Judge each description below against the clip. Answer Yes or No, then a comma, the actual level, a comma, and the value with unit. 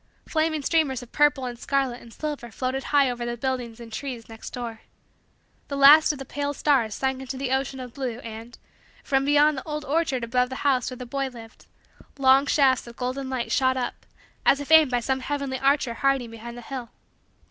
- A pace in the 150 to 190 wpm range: No, fast, 205 wpm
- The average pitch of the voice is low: No, very high, 265 Hz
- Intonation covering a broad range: No, narrow, 2.6 semitones